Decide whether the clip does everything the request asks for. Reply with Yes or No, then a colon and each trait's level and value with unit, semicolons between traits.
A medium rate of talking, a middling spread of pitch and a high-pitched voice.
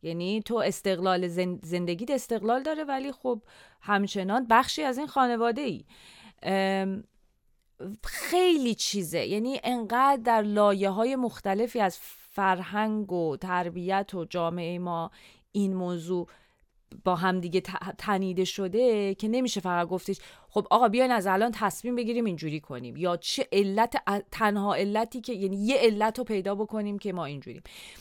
Yes: average, 145 wpm; average, 4.0 semitones; high, 205 Hz